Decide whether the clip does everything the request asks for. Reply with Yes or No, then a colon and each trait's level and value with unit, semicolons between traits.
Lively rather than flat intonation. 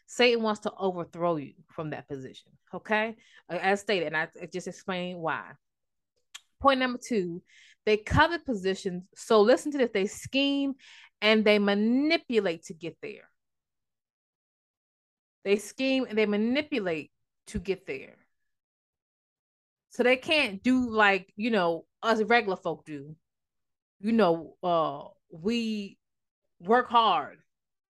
Yes: wide, 5.7 semitones